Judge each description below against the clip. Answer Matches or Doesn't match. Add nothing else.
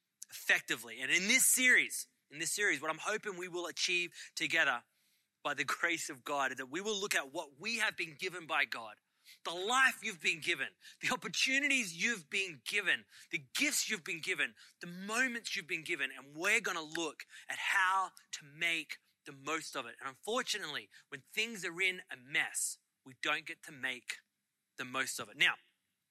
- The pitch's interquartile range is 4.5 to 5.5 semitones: Matches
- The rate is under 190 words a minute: Doesn't match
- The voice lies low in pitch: Doesn't match